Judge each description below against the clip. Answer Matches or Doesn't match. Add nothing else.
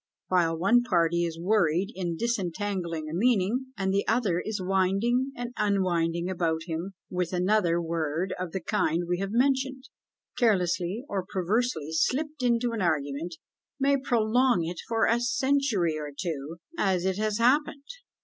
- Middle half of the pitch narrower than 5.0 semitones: Doesn't match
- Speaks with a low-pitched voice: Doesn't match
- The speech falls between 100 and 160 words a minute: Matches